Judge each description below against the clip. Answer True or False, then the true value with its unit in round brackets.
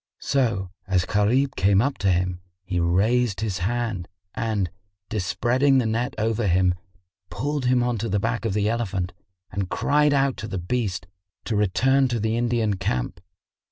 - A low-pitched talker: True (110 Hz)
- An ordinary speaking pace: True (165 wpm)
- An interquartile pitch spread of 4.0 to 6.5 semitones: True (4.4 semitones)